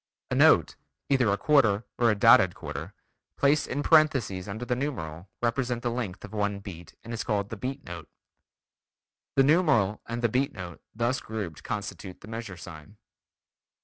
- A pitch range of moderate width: Yes, average, 4.2 semitones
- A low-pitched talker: Yes, low, 110 Hz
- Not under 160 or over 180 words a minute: Yes, average, 170 wpm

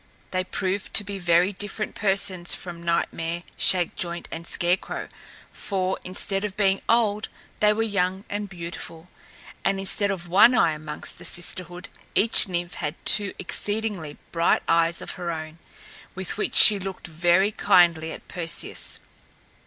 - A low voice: No, medium, 185 Hz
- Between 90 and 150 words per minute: Yes, average, 145 wpm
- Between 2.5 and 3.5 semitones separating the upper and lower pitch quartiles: Yes, average, 2.8 semitones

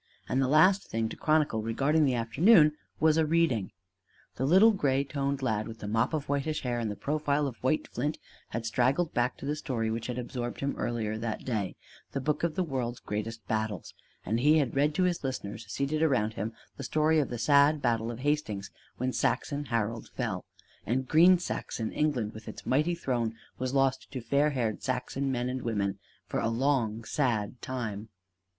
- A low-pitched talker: Yes, low, 130 Hz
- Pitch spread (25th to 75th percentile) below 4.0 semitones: No, average, 4.6 semitones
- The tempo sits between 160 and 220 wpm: Yes, average, 195 wpm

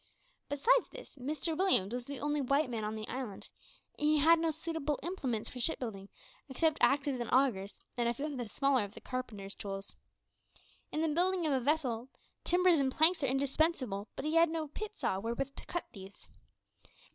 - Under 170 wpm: No, average, 190 wpm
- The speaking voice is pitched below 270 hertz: No, very high, 275 Hz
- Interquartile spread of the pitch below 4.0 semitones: No, average, 5.1 semitones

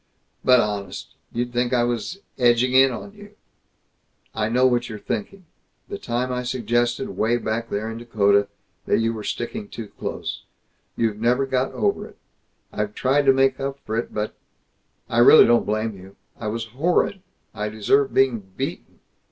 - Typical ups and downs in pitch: Yes, average, 3.1 semitones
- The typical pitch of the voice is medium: No, low, 120 Hz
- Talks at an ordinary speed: Yes, average, 175 wpm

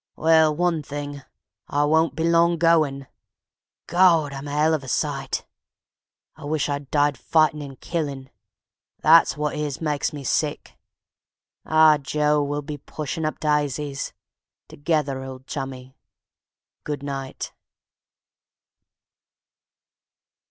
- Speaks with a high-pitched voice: No, medium, 150 Hz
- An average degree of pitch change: No, narrow, 2.1 semitones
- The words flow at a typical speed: No, slow, 115 wpm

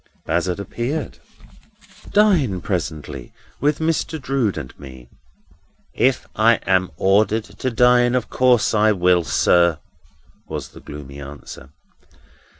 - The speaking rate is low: Yes, slow, 115 wpm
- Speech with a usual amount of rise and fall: No, wide, 6.6 semitones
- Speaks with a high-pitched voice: No, low, 105 Hz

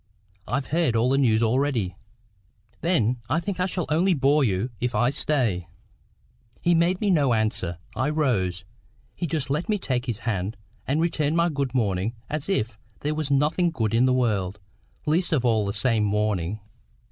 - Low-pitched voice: Yes, low, 130 Hz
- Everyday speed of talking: Yes, average, 180 wpm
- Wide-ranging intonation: Yes, wide, 6.0 semitones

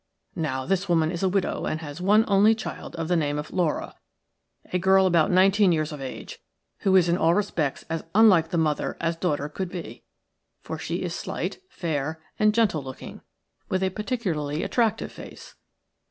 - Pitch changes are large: No, average, 3.6 semitones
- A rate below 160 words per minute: No, average, 185 wpm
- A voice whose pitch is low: No, medium, 175 Hz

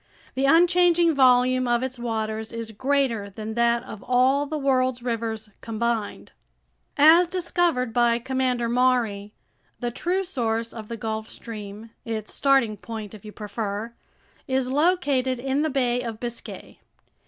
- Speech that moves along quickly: No, average, 140 wpm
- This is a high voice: Yes, high, 240 Hz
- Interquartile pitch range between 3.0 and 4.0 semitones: Yes, average, 3.3 semitones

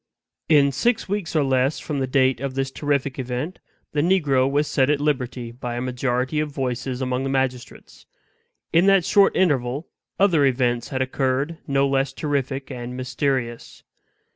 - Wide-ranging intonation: No, narrow, 2.5 semitones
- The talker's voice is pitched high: No, low, 135 Hz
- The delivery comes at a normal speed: Yes, average, 165 wpm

